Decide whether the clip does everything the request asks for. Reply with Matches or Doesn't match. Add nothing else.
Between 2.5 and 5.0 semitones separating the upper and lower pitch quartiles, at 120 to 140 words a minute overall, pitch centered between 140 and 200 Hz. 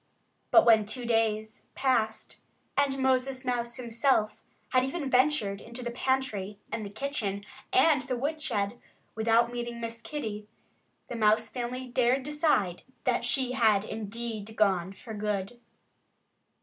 Doesn't match